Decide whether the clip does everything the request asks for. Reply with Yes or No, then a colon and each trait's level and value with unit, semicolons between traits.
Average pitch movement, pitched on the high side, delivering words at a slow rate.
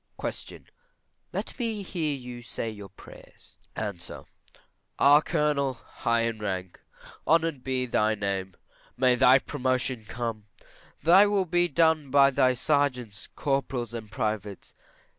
No: average, 4.9 semitones; low, 130 Hz; slow, 125 wpm